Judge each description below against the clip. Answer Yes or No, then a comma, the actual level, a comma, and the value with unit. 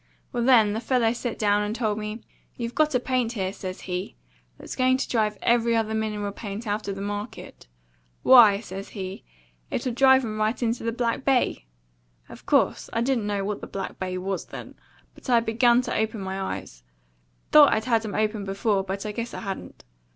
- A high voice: Yes, high, 220 Hz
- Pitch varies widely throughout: No, average, 3.0 semitones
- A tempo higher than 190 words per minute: Yes, average, 200 wpm